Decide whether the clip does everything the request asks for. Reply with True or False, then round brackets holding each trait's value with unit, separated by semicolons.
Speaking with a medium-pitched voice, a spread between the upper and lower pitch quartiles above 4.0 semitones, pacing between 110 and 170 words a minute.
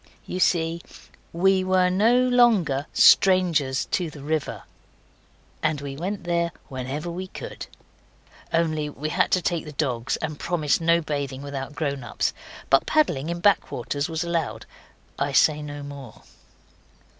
False (160 Hz; 3.7 semitones; 150 wpm)